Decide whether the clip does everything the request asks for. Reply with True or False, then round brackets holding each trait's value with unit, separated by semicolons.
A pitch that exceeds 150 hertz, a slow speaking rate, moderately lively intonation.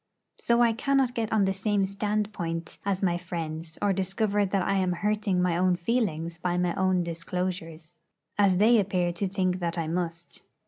False (185 Hz; 180 wpm; 3.0 semitones)